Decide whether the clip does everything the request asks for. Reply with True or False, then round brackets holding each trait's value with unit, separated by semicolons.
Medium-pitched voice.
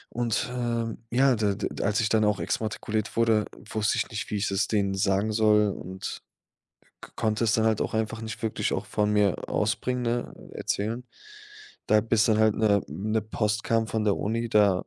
False (110 Hz)